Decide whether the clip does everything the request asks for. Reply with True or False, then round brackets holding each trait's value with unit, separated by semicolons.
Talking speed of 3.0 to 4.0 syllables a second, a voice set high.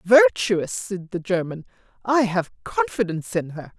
False (4.4 syllables/s; 195 Hz)